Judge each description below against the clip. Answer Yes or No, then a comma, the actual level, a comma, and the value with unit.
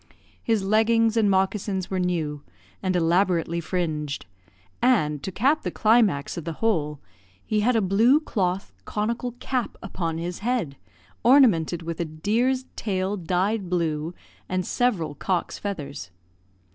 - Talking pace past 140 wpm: No, slow, 135 wpm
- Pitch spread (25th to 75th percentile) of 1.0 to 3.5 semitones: No, average, 5.1 semitones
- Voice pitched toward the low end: No, high, 190 Hz